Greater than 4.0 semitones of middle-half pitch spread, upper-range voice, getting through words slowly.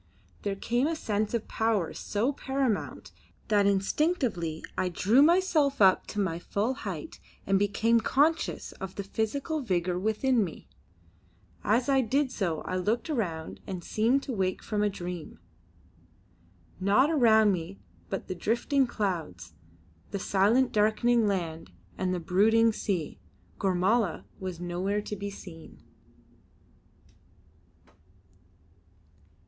Yes: average, 4.5 semitones; high, 205 Hz; slow, 125 wpm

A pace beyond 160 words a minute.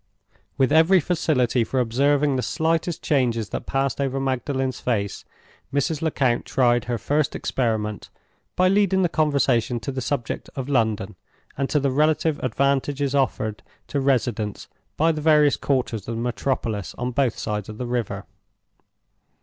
No: average, 150 wpm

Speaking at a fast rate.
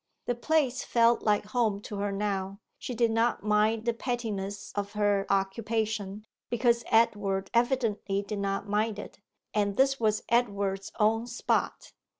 No: average, 150 wpm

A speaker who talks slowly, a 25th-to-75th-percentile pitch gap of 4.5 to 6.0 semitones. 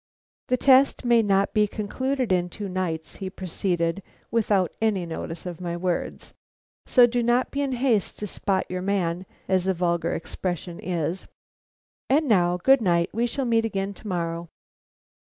No: average, 165 wpm; average, 4.8 semitones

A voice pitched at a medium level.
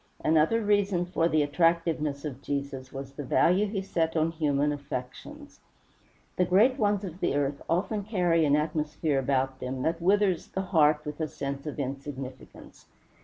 Yes: medium, 155 Hz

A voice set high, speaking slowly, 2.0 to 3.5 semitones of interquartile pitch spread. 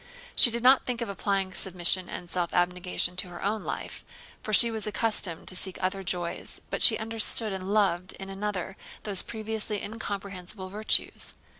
No: high, 195 Hz; average, 170 wpm; average, 3.0 semitones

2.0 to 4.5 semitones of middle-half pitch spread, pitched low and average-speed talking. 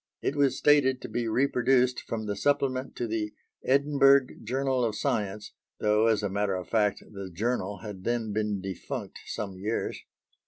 Yes: average, 4.2 semitones; low, 115 Hz; average, 165 wpm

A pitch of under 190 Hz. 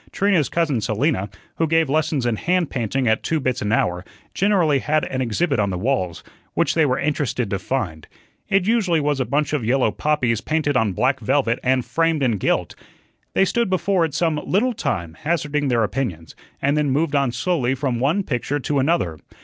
Yes: medium, 140 Hz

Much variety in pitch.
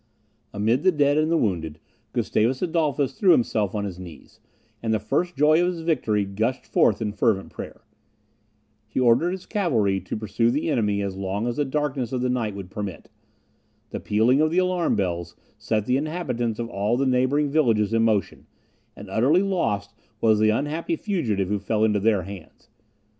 Yes: wide, 6.3 semitones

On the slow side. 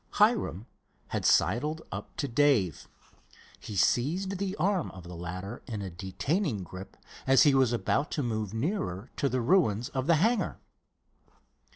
No: average, 155 wpm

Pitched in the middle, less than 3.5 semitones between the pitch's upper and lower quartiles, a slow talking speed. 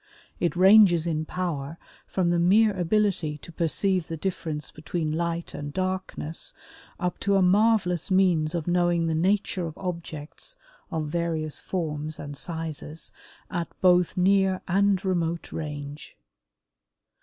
Yes: medium, 170 Hz; average, 2.9 semitones; slow, 130 wpm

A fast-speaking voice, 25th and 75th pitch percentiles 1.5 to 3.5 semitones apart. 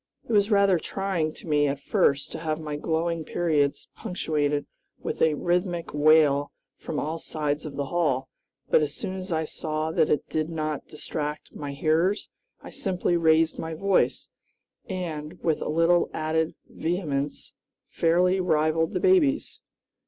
No: average, 155 wpm; narrow, 2.6 semitones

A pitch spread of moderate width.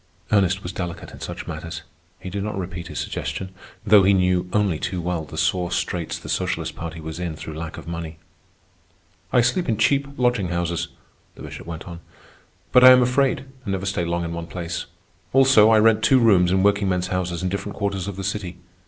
Yes: average, 3.5 semitones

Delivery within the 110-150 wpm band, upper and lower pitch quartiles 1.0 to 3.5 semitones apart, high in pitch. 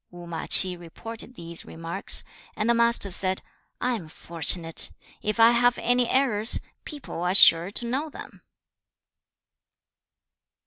No: average, 140 wpm; wide, 5.6 semitones; high, 205 Hz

